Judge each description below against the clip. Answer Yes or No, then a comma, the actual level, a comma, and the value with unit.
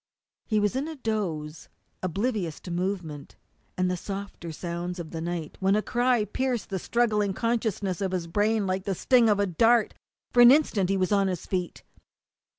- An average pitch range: Yes, average, 4.0 semitones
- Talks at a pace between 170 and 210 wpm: Yes, average, 185 wpm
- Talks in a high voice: Yes, high, 195 Hz